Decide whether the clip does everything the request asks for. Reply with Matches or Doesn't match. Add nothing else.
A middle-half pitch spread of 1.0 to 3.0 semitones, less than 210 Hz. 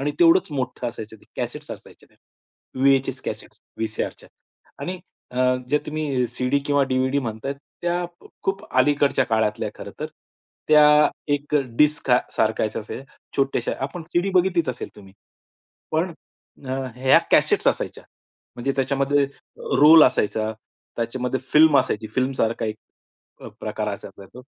Doesn't match